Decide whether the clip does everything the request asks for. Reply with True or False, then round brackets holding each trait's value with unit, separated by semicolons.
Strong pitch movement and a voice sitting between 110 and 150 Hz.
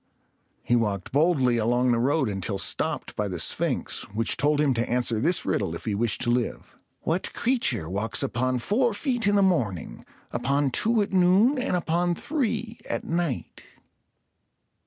True (8.2 semitones; 135 Hz)